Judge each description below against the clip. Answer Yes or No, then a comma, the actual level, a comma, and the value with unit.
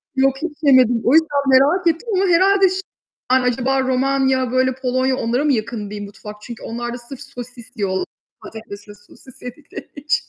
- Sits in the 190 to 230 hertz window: No, very high, 260 Hz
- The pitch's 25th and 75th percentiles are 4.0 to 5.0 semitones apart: No, average, 2.9 semitones